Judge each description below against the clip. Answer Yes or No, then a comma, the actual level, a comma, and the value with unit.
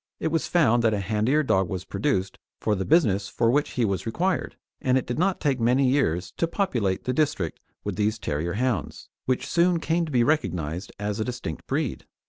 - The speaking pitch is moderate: No, low, 120 Hz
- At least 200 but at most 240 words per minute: Yes, fast, 205 wpm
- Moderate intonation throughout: No, wide, 7.0 semitones